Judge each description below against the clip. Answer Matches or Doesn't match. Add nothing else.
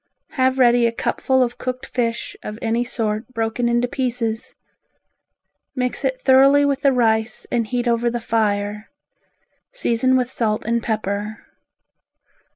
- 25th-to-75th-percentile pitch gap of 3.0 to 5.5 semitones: Doesn't match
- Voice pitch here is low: Doesn't match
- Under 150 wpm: Matches